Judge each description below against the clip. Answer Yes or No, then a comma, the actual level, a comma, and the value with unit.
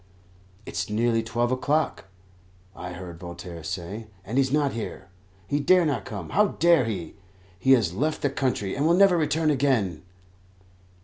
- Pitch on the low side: Yes, low, 120 Hz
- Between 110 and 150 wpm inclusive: No, average, 165 wpm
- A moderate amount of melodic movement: No, wide, 7.5 semitones